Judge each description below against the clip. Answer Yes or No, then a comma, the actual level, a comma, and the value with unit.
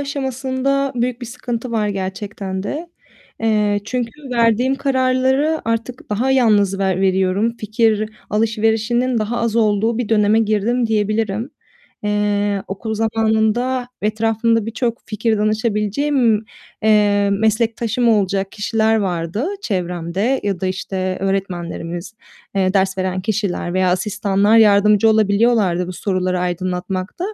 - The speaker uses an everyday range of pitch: Yes, average, 3.0 semitones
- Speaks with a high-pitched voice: Yes, high, 215 Hz